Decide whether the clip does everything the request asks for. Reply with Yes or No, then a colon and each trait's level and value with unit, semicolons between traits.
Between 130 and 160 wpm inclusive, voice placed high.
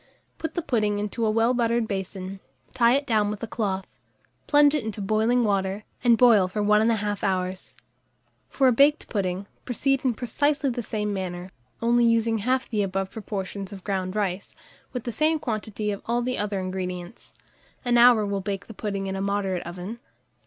No: average, 185 wpm; high, 210 Hz